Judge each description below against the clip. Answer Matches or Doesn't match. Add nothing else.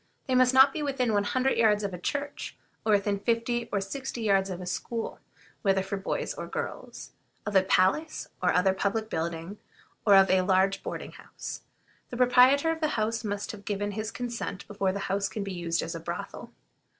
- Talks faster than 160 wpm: Matches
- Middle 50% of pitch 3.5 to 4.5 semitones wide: Matches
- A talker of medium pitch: Doesn't match